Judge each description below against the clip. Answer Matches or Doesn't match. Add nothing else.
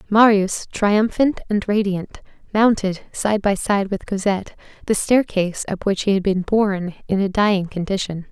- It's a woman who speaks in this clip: Matches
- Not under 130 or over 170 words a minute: Matches